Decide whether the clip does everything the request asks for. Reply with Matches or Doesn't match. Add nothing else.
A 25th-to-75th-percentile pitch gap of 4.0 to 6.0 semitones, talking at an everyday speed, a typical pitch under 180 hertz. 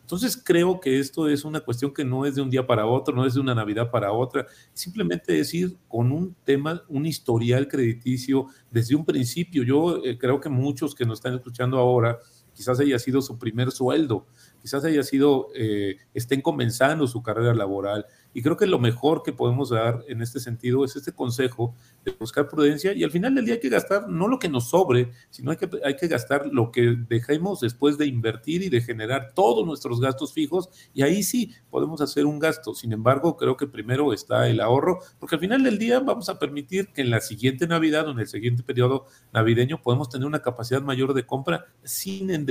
Doesn't match